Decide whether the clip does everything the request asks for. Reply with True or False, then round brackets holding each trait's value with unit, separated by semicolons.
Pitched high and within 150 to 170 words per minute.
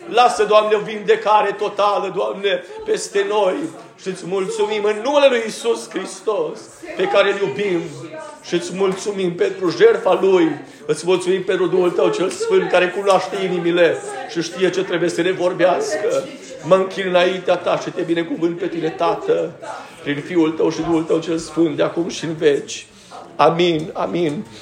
True (200 Hz; 165 wpm)